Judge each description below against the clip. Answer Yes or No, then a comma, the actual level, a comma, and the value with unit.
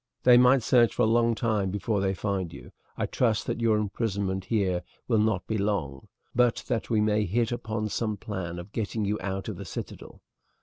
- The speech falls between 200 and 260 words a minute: Yes, fast, 205 wpm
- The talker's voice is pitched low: Yes, low, 105 Hz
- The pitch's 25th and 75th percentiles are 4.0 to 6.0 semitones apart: No, average, 3.0 semitones